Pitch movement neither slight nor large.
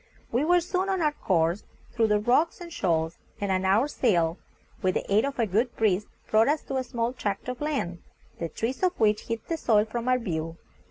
No: wide, 6.1 semitones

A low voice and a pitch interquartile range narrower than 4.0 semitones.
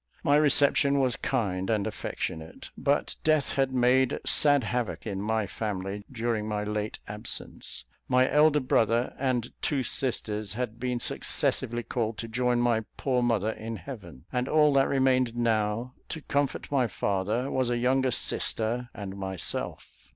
Yes: low, 120 Hz; average, 3.5 semitones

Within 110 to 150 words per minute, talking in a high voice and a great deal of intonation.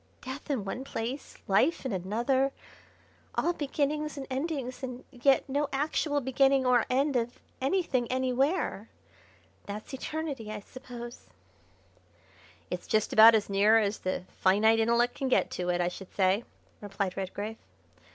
No: average, 140 wpm; high, 245 Hz; average, 4.3 semitones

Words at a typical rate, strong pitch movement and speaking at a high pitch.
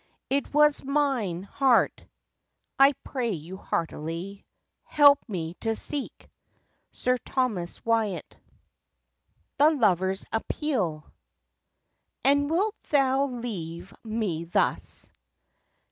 No: slow, 90 wpm; wide, 7.2 semitones; high, 230 Hz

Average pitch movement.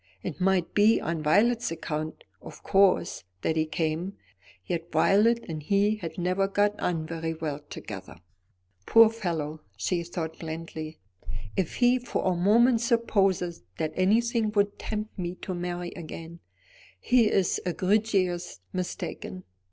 Yes: average, 4.3 semitones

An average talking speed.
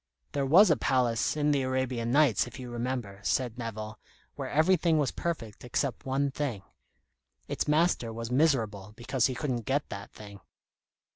Yes: average, 165 wpm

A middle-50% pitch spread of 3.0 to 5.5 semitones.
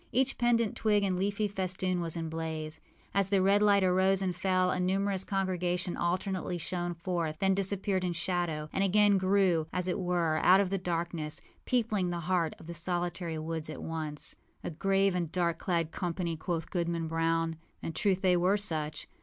No: narrow, 2.6 semitones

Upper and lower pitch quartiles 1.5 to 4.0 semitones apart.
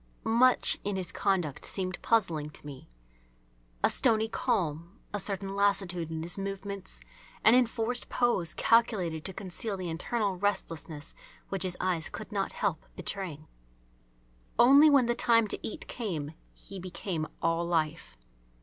No: average, 4.8 semitones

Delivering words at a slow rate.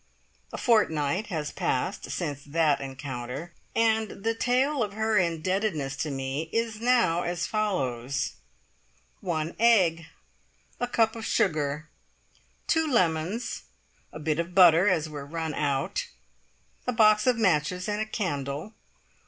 Yes: slow, 130 wpm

